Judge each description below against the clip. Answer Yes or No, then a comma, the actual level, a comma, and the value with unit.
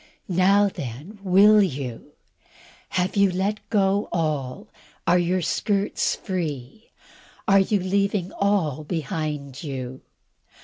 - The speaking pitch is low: No, medium, 185 Hz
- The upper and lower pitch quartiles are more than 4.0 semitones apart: Yes, average, 5.1 semitones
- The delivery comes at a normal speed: No, slow, 105 wpm